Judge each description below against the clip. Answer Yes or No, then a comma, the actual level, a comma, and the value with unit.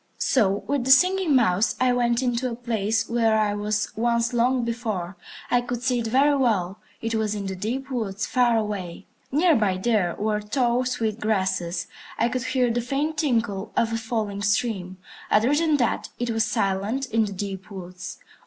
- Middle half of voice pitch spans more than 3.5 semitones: No, average, 3.2 semitones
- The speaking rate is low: No, average, 185 wpm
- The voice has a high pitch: Yes, high, 225 Hz